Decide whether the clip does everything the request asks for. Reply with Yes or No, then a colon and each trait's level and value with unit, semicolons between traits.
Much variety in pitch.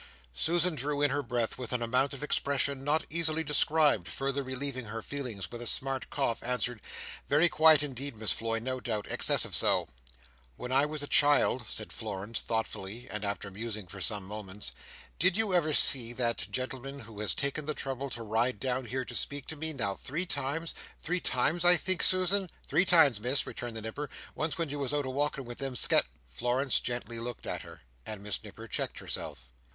No: average, 4.3 semitones